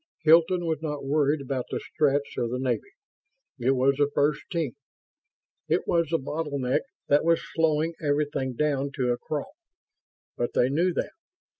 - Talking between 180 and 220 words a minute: No, average, 160 wpm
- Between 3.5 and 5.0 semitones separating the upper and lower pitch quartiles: No, average, 3.0 semitones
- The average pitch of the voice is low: No, medium, 145 Hz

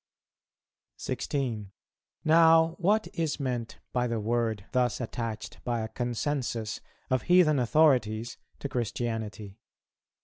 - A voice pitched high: No, low, 120 Hz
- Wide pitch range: No, average, 4.7 semitones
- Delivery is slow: Yes, slow, 110 wpm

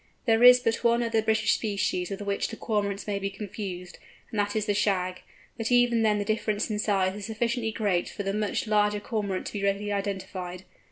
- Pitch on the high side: Yes, high, 210 Hz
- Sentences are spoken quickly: Yes, fast, 210 wpm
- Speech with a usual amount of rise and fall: No, narrow, 2.0 semitones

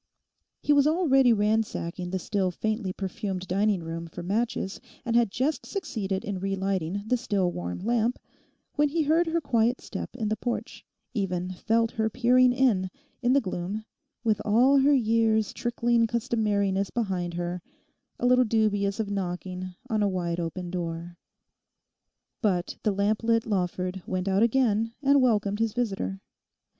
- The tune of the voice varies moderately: Yes, average, 4.1 semitones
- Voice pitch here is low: No, high, 210 Hz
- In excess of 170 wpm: No, average, 155 wpm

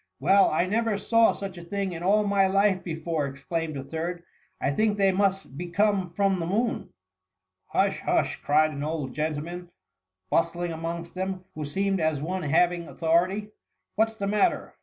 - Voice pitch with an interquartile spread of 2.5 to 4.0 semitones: Yes, average, 3.5 semitones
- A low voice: No, medium, 180 Hz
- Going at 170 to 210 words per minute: Yes, average, 195 wpm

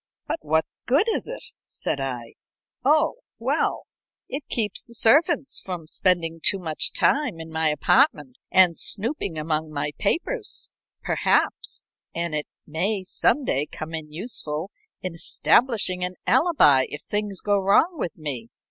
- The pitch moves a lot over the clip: Yes, wide, 8.2 semitones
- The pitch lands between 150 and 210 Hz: Yes, medium, 185 Hz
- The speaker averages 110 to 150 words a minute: Yes, average, 140 wpm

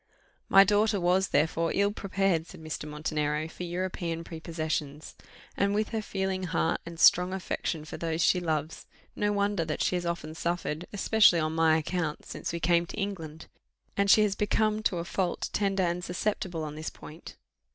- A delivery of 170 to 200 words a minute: Yes, average, 180 wpm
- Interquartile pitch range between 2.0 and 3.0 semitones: No, average, 3.4 semitones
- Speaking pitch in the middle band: Yes, medium, 175 Hz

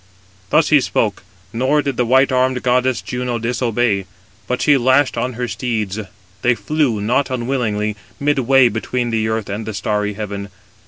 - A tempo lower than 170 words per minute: Yes, average, 160 wpm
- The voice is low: Yes, low, 120 Hz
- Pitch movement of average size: Yes, average, 3.1 semitones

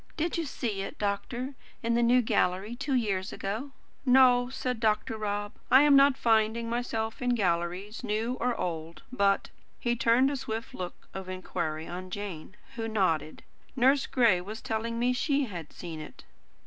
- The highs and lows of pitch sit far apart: No, average, 4.4 semitones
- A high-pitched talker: Yes, high, 225 Hz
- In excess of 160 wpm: Yes, average, 170 wpm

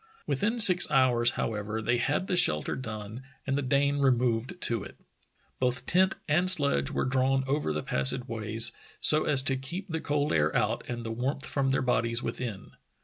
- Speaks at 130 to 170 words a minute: No, average, 180 wpm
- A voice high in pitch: No, low, 130 Hz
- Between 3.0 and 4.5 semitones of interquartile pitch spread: Yes, average, 4.1 semitones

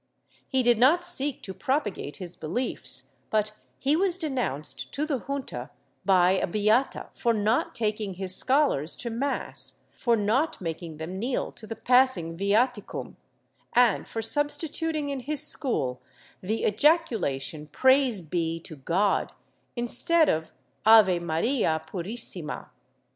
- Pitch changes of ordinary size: No, wide, 7.1 semitones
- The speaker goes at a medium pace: No, slow, 130 wpm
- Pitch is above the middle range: Yes, high, 225 Hz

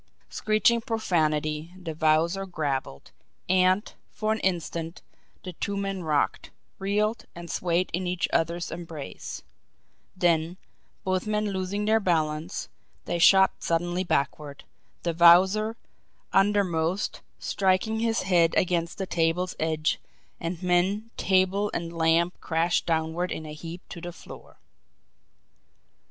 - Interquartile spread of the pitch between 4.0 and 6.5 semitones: No, average, 2.8 semitones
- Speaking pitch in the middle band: Yes, medium, 175 Hz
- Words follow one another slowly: Yes, slow, 120 wpm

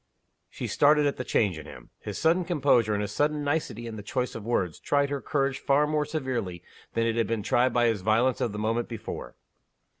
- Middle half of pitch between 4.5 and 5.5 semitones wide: Yes, average, 4.9 semitones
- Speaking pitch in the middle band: No, low, 120 Hz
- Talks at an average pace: No, fast, 220 wpm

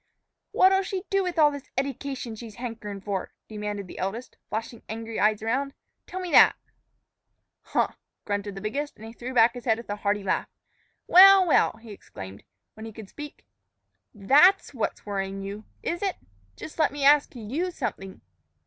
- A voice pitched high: Yes, high, 230 Hz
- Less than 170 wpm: No, average, 175 wpm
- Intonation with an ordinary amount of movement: No, wide, 5.9 semitones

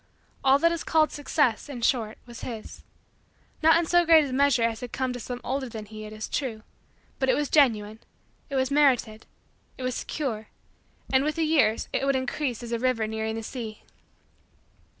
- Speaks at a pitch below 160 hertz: No, very high, 255 Hz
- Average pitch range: Yes, average, 4.2 semitones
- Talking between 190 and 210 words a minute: Yes, average, 195 wpm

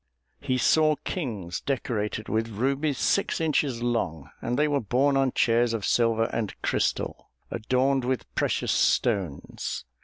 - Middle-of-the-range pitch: No, low, 120 Hz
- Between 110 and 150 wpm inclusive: Yes, average, 140 wpm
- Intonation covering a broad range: No, average, 3.7 semitones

